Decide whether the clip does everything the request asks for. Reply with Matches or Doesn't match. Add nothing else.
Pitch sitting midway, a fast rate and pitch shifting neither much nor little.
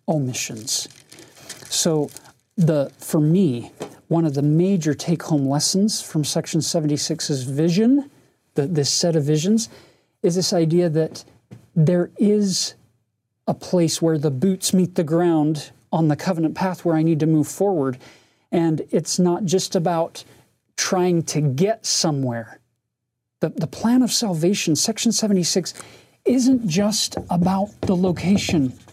Doesn't match